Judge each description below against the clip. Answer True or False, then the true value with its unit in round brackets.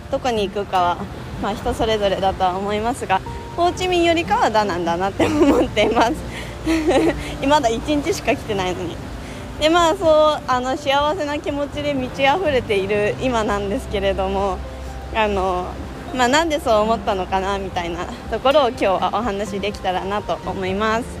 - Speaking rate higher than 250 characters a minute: True (350 characters per minute)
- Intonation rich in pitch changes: True (7.0 semitones)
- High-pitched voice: True (215 Hz)